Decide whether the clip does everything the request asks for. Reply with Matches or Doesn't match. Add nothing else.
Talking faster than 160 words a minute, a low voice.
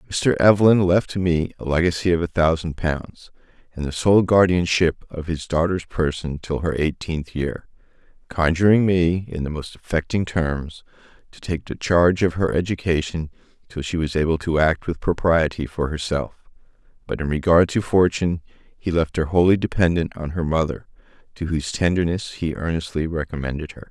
Matches